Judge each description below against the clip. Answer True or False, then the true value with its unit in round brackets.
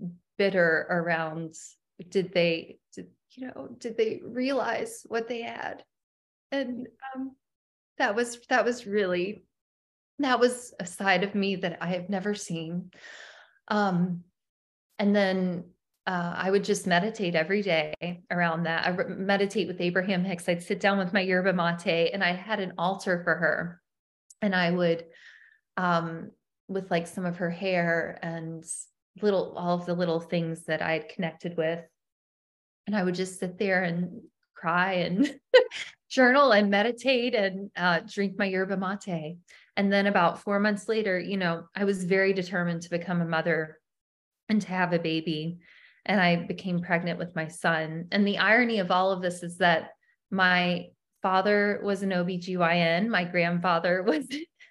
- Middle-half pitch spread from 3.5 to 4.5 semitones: False (3.0 semitones)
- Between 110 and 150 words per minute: False (160 wpm)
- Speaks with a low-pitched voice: False (185 Hz)